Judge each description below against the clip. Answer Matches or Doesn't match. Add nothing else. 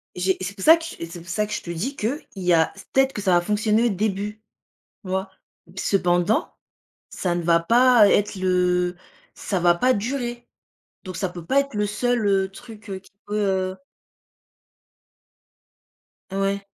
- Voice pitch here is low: Doesn't match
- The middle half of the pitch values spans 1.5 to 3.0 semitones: Doesn't match